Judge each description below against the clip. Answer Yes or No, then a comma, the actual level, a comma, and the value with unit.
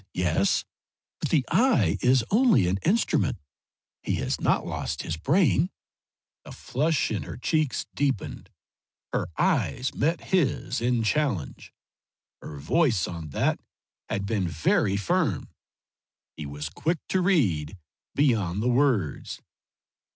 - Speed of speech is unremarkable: No, slow, 130 wpm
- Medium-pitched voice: No, low, 120 Hz